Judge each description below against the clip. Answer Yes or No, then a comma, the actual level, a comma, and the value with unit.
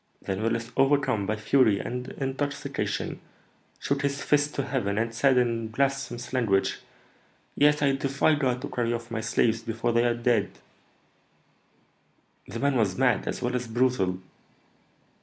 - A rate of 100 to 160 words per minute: Yes, average, 150 wpm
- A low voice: Yes, low, 125 Hz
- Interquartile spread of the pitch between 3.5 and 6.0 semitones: No, average, 3.1 semitones